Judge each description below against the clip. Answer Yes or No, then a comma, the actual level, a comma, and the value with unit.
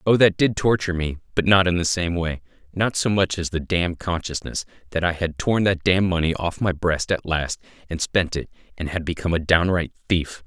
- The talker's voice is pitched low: Yes, very low, 90 Hz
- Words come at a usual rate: No, fast, 225 wpm